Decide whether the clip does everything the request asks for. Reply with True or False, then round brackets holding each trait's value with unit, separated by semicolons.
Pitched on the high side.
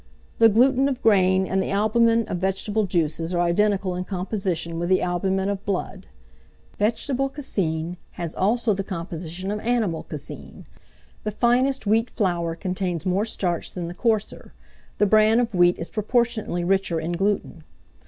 True (195 Hz)